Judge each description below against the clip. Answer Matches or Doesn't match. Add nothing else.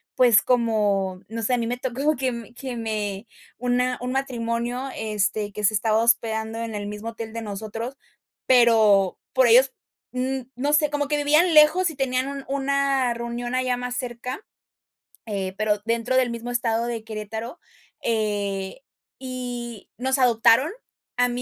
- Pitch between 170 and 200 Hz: Doesn't match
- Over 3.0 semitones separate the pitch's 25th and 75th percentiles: Doesn't match